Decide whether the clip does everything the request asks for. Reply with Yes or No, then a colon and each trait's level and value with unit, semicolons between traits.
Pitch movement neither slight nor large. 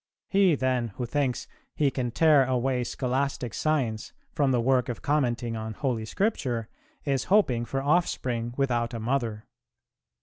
Yes: average, 3.0 semitones